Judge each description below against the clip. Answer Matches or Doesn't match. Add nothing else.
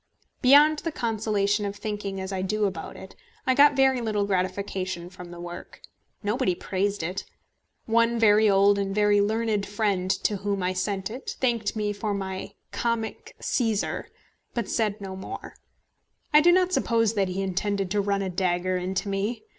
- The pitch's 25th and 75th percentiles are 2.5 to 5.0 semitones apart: Matches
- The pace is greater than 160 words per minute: Matches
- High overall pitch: Matches